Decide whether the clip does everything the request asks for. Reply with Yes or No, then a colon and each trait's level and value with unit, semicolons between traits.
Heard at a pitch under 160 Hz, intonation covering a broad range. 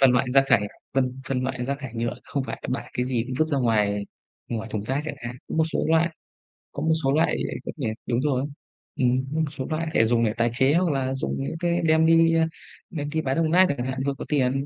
No: low, 135 Hz; average, 4.2 semitones